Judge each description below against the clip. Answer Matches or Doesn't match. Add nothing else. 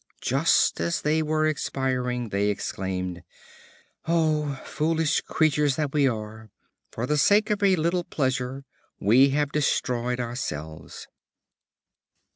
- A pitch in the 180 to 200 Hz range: Doesn't match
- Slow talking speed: Matches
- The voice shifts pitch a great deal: Doesn't match